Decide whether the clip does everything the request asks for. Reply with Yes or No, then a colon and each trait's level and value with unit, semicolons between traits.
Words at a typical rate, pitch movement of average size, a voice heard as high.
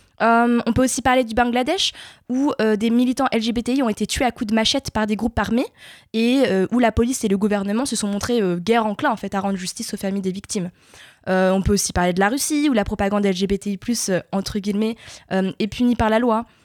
No: fast, 240 wpm; average, 3.3 semitones; high, 220 Hz